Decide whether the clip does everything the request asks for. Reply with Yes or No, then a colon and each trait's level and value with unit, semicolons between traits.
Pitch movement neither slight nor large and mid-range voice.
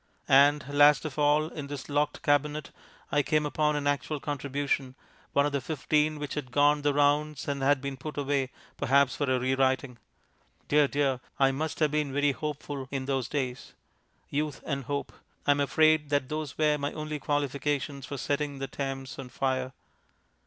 No: narrow, 1.6 semitones; medium, 145 Hz